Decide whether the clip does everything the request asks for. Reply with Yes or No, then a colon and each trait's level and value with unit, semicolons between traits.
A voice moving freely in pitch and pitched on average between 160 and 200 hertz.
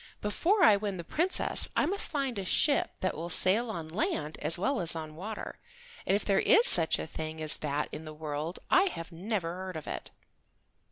Yes: wide, 5.7 semitones; medium, 185 Hz